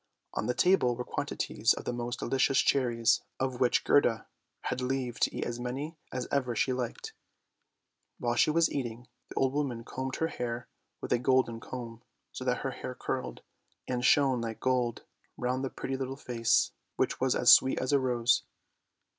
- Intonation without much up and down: Yes, narrow, 1.8 semitones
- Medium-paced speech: Yes, average, 180 wpm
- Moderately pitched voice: No, low, 125 Hz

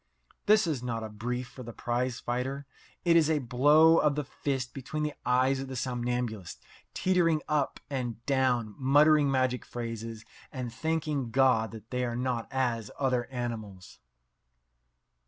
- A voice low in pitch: Yes, low, 125 Hz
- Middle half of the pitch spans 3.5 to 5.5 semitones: No, average, 3.1 semitones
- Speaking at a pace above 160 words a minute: No, average, 155 wpm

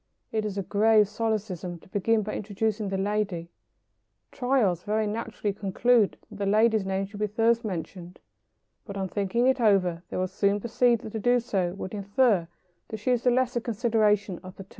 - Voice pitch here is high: Yes, high, 210 Hz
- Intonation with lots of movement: No, average, 2.8 semitones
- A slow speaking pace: No, average, 190 wpm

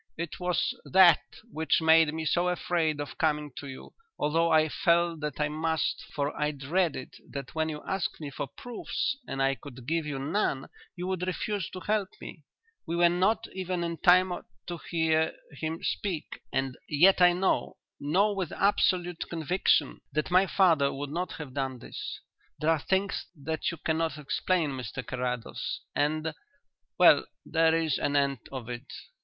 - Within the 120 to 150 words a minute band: No, average, 170 wpm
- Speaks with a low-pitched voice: No, medium, 160 Hz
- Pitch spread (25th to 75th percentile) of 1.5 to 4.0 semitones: Yes, average, 3.6 semitones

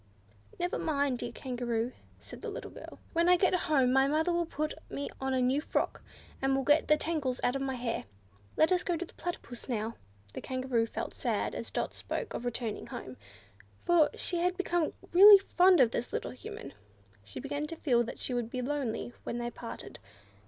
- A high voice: Yes, very high, 270 Hz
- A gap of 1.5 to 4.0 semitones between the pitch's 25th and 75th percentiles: No, average, 5.3 semitones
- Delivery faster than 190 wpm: Yes, average, 200 wpm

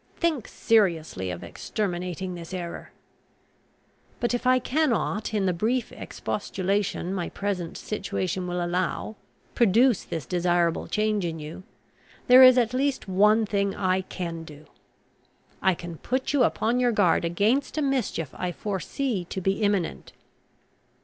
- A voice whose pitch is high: Yes, high, 195 Hz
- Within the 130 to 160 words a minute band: Yes, average, 140 wpm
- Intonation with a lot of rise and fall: No, average, 5.0 semitones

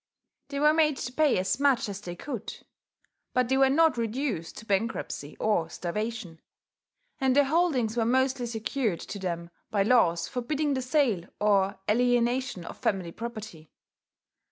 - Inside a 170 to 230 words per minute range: No, average, 155 wpm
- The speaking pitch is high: Yes, high, 235 Hz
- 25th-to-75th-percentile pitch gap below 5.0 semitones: No, average, 5.3 semitones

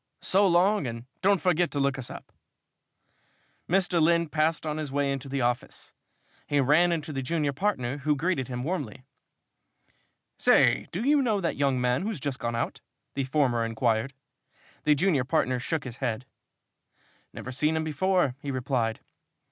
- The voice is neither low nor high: Yes, medium, 145 Hz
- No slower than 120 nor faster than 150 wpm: No, average, 165 wpm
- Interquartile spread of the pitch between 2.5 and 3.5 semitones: No, average, 4.8 semitones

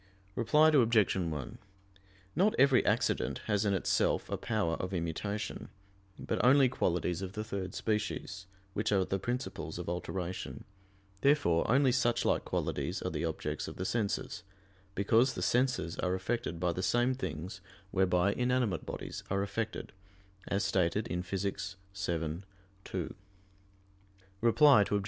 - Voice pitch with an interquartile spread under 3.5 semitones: No, average, 4.9 semitones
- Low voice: Yes, low, 100 Hz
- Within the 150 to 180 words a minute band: No, average, 140 wpm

